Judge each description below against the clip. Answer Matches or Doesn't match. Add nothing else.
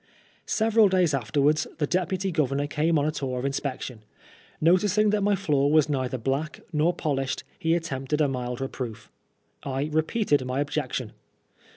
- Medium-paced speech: Matches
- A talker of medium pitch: Matches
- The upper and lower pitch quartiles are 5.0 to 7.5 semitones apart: Doesn't match